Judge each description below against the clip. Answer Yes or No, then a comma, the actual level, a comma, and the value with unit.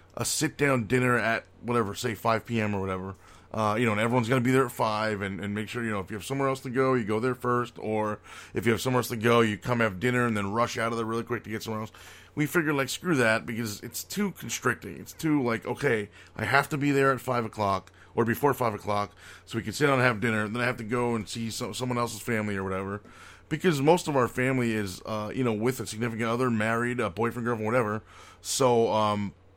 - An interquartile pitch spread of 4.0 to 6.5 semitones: No, average, 2.9 semitones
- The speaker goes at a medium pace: No, fast, 265 wpm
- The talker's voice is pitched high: No, low, 115 Hz